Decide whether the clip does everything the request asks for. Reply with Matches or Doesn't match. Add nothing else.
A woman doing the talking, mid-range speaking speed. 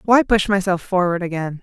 Matches